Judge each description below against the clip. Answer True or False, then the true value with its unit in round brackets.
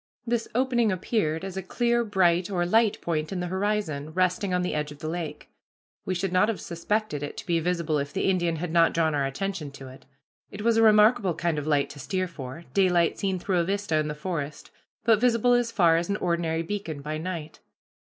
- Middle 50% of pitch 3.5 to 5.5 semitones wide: True (4.4 semitones)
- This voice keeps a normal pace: False (220 wpm)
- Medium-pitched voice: True (175 Hz)